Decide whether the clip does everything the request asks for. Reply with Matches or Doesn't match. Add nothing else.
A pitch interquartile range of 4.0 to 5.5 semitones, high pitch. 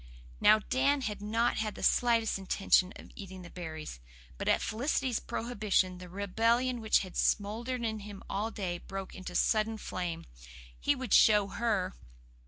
Doesn't match